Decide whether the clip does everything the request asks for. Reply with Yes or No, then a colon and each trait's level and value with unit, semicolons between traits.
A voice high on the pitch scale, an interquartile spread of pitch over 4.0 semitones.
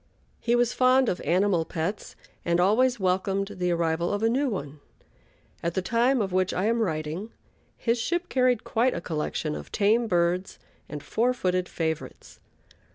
Yes: high, 195 Hz; wide, 5.4 semitones